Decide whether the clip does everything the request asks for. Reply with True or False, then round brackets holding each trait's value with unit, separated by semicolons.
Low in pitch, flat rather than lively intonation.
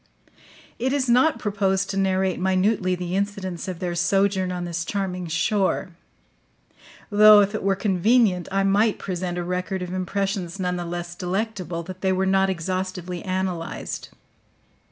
False (190 Hz; 1.7 semitones)